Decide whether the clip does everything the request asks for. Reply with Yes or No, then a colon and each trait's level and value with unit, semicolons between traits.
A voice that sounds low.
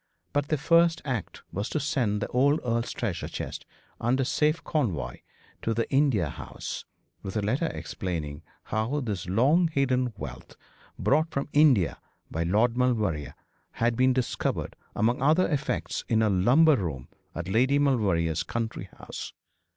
Yes: low, 120 Hz